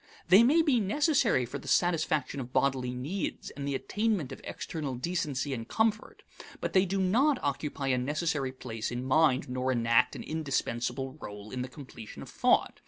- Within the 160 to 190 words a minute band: Yes, average, 175 wpm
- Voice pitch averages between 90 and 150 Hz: Yes, medium, 140 Hz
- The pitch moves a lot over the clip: Yes, wide, 6.4 semitones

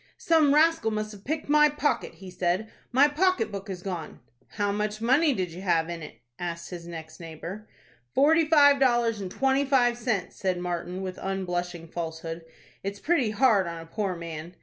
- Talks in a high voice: Yes, high, 200 Hz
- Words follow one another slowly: No, average, 185 wpm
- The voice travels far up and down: Yes, wide, 7.2 semitones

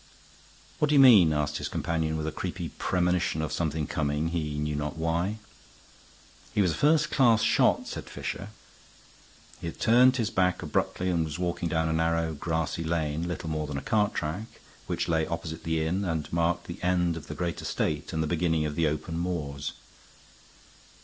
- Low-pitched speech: Yes, very low, 85 Hz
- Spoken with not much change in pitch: Yes, narrow, 2.3 semitones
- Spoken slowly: No, average, 190 wpm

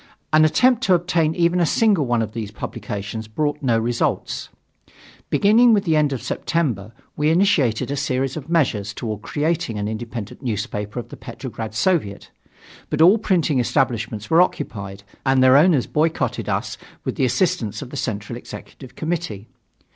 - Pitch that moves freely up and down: Yes, wide, 6.9 semitones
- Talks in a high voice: No, low, 135 Hz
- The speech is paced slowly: No, average, 160 wpm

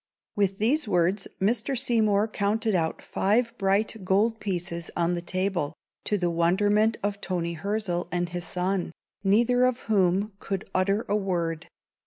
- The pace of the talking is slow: No, average, 150 wpm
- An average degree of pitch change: Yes, average, 3.4 semitones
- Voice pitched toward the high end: Yes, high, 195 Hz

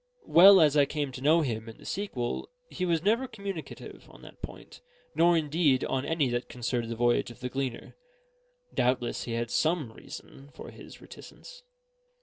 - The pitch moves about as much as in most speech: No, wide, 5.7 semitones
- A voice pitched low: No, medium, 145 Hz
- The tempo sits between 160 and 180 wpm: Yes, average, 175 wpm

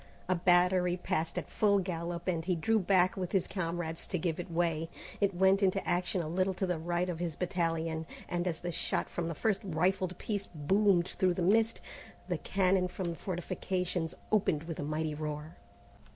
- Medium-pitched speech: Yes, medium, 175 Hz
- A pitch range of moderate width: No, narrow, 2.3 semitones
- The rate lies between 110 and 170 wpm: No, average, 195 wpm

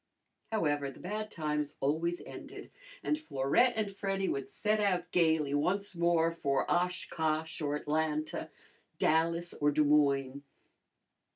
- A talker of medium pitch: Yes, medium, 160 Hz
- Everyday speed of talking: No, slow, 125 wpm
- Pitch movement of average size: Yes, average, 3.6 semitones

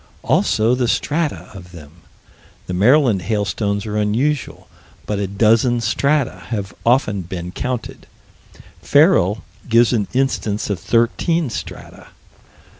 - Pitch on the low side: Yes, low, 110 Hz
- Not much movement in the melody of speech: No, average, 4.2 semitones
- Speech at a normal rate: No, slow, 115 wpm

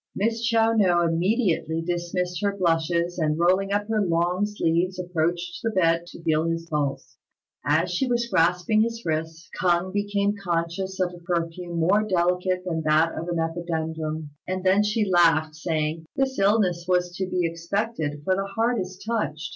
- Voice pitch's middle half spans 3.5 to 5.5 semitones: No, average, 3.1 semitones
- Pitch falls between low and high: Yes, medium, 175 Hz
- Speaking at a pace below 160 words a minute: No, average, 170 wpm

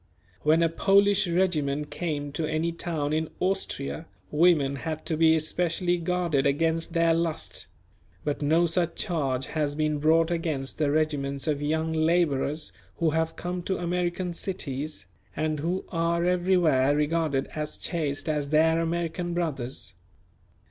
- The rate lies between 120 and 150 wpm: Yes, average, 140 wpm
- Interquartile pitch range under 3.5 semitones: Yes, narrow, 2.5 semitones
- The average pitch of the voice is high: No, medium, 160 Hz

